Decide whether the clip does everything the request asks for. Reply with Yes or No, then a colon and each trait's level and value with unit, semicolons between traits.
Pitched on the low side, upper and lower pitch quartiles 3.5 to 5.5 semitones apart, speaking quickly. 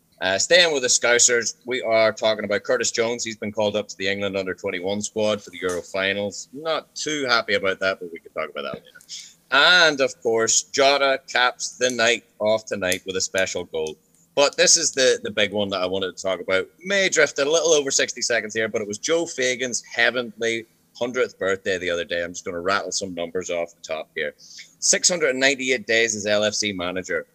Yes: low, 110 Hz; average, 4.9 semitones; fast, 215 wpm